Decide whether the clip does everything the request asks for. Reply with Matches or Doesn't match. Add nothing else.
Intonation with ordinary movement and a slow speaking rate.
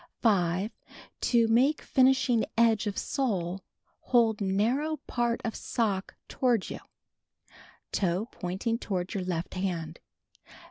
Matches